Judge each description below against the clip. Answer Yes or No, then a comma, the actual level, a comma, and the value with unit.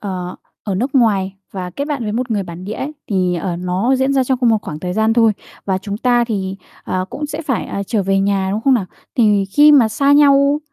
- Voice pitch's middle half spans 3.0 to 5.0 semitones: No, wide, 5.4 semitones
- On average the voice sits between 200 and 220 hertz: Yes, high, 215 Hz